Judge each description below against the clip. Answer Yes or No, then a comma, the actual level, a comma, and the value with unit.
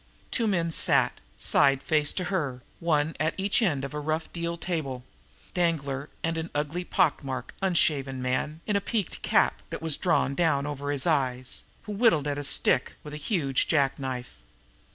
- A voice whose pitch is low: No, medium, 150 Hz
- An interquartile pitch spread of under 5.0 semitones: Yes, average, 3.6 semitones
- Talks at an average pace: Yes, average, 180 wpm